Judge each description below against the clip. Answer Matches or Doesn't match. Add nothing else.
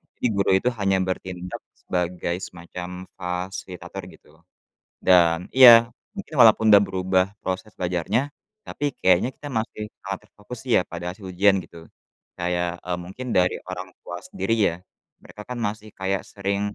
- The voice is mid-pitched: Doesn't match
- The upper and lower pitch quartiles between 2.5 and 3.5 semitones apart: Matches